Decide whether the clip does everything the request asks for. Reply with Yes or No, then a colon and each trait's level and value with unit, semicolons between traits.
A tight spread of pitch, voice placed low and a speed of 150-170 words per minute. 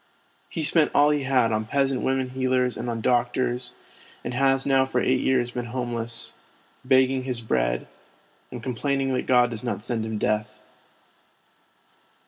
Yes: narrow, 2.0 semitones; low, 125 Hz; average, 160 wpm